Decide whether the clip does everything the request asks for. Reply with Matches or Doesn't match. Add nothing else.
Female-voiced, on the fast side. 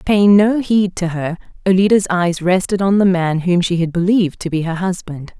Matches